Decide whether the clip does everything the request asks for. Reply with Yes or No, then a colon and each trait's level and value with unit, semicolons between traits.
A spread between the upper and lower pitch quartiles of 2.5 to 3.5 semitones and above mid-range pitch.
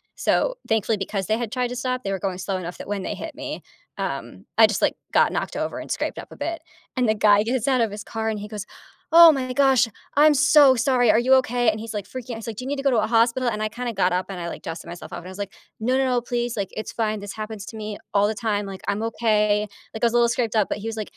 Yes: average, 3.2 semitones; high, 220 Hz